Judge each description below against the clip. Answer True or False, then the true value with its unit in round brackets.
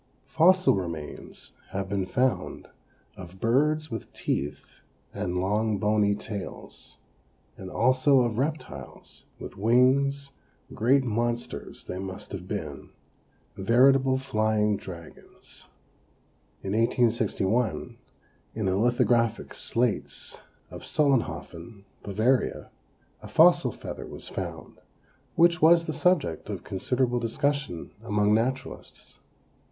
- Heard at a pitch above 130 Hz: False (115 Hz)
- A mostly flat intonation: False (4.9 semitones)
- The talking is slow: True (105 wpm)